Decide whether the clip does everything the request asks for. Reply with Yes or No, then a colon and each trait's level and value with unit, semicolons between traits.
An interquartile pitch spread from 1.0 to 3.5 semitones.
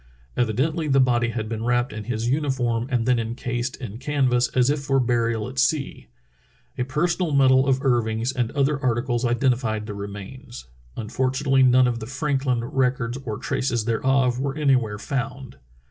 Yes: narrow, 2.4 semitones